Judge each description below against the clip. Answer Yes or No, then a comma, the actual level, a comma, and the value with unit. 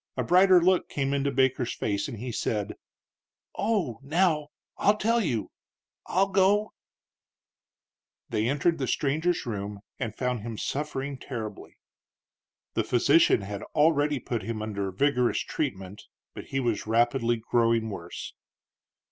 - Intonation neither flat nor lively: No, wide, 5.7 semitones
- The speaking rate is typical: No, slow, 130 wpm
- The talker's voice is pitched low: Yes, low, 130 Hz